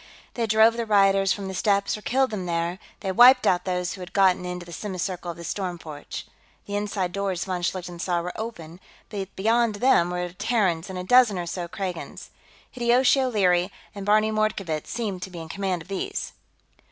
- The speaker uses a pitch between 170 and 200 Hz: Yes, high, 190 Hz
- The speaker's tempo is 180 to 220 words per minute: Yes, average, 200 wpm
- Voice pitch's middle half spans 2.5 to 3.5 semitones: Yes, average, 3.2 semitones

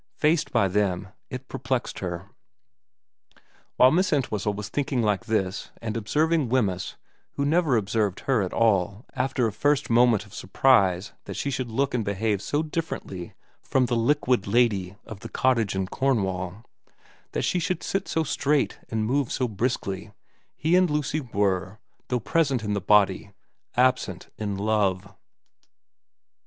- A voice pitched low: Yes, low, 115 Hz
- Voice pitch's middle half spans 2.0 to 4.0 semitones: No, average, 5.1 semitones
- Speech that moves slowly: No, average, 150 wpm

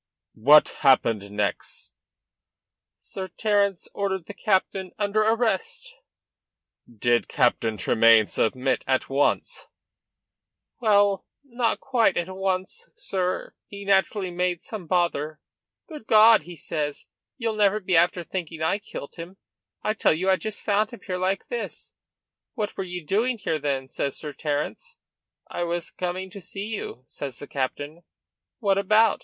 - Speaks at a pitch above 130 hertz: Yes, medium, 185 Hz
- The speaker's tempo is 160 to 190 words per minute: No, average, 140 wpm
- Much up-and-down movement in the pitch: Yes, wide, 5.7 semitones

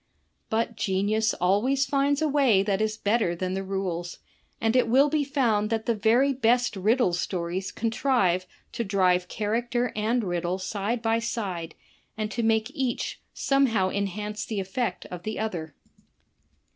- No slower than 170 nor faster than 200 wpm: No, average, 155 wpm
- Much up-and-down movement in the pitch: No, average, 4.0 semitones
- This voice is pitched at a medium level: No, high, 215 Hz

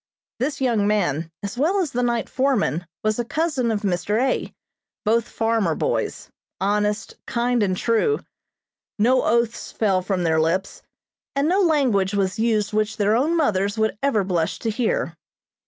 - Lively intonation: No, average, 4.0 semitones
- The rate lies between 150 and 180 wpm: Yes, average, 160 wpm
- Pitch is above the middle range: Yes, high, 220 Hz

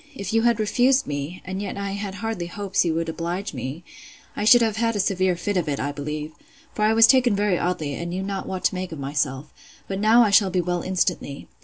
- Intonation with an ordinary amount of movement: Yes, average, 3.9 semitones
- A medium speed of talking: No, fast, 240 wpm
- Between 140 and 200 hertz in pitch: Yes, medium, 185 Hz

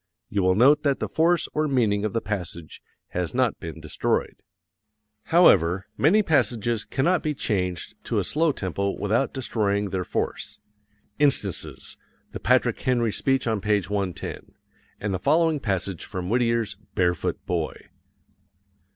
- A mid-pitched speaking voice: No, low, 110 Hz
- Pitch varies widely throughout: Yes, wide, 5.9 semitones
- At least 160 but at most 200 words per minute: No, average, 140 wpm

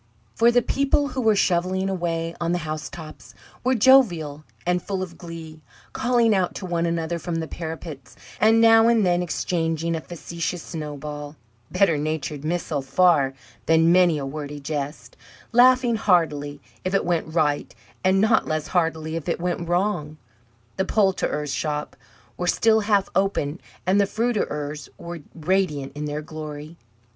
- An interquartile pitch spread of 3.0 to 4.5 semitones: Yes, average, 3.9 semitones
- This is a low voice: No, medium, 170 Hz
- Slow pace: No, average, 155 wpm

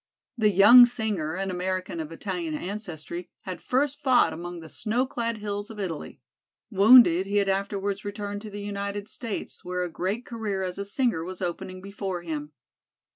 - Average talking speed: Yes, average, 175 wpm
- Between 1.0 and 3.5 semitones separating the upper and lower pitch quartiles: Yes, average, 2.9 semitones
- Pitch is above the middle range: Yes, high, 200 Hz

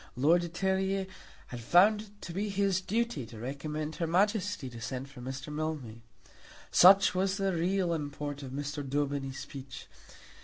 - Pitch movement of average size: No, wide, 5.7 semitones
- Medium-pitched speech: Yes, medium, 155 Hz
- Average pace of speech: Yes, average, 160 wpm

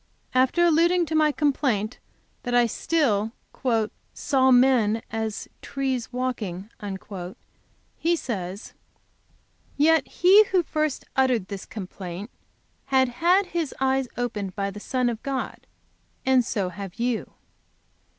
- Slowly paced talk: Yes, slow, 120 wpm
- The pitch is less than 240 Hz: No, very high, 255 Hz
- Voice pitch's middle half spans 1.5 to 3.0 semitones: No, wide, 5.6 semitones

